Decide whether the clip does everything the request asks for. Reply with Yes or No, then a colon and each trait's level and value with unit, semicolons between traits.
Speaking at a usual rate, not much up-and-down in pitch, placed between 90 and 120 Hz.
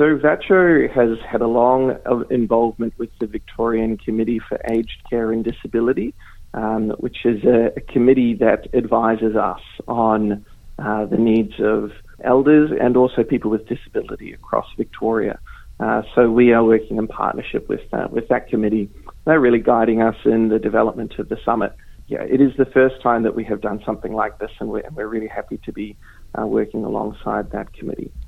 Yes: average, 180 wpm; narrow, 1.9 semitones; low, 115 Hz